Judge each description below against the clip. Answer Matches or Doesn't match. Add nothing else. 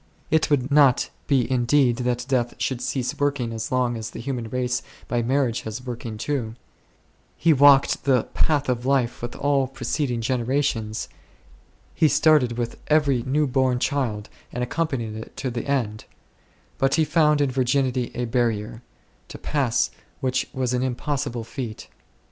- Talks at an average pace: Matches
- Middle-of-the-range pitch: Doesn't match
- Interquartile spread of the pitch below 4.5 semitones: Matches